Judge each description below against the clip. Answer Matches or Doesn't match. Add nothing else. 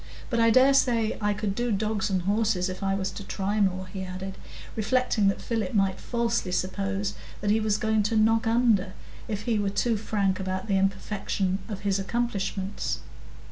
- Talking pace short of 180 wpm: Doesn't match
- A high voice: Matches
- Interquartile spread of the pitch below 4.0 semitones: Matches